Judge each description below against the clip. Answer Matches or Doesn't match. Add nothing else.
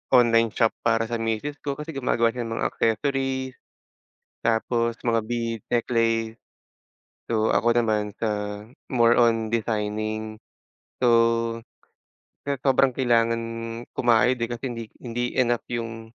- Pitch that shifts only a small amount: Matches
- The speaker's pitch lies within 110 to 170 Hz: Matches